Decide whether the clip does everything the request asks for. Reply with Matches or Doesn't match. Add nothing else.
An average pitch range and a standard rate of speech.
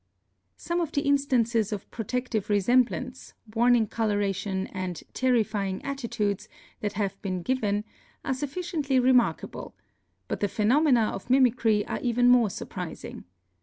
Doesn't match